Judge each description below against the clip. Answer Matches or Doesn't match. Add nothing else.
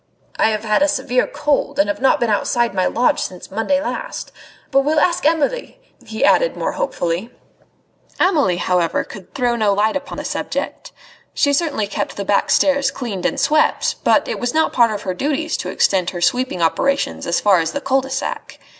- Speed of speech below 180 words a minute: Doesn't match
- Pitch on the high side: Matches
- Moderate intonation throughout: Doesn't match